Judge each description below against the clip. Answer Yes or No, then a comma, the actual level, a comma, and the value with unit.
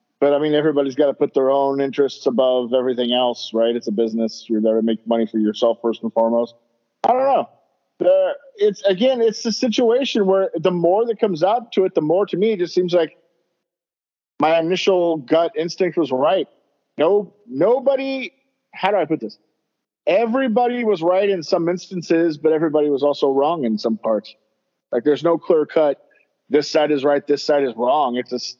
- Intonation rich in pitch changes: Yes, wide, 7.6 semitones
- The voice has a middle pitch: Yes, medium, 160 Hz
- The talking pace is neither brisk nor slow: Yes, average, 195 wpm